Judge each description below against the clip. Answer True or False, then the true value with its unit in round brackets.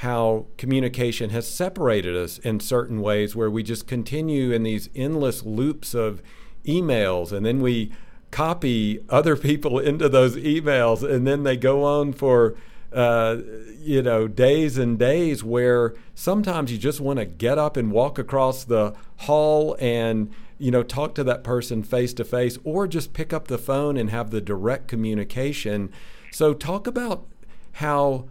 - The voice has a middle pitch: False (125 Hz)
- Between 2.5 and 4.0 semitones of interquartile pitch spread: False (4.4 semitones)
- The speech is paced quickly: False (165 wpm)